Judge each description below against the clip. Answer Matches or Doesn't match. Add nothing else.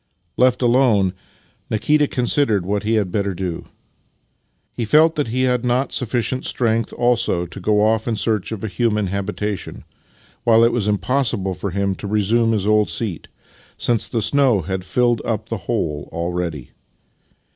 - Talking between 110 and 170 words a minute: Matches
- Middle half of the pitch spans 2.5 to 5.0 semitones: Matches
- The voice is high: Doesn't match